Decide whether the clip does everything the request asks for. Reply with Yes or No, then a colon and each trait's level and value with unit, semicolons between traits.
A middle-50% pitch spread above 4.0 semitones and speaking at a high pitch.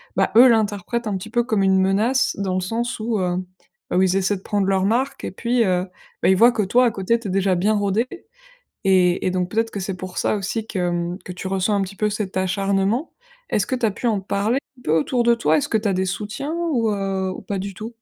No: average, 3.2 semitones; high, 200 Hz